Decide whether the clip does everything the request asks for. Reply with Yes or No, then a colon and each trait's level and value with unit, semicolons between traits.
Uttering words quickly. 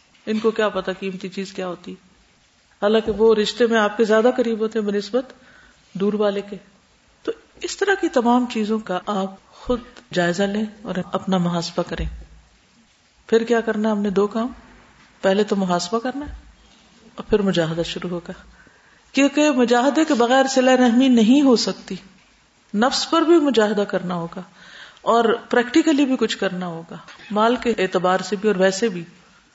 No: average, 175 wpm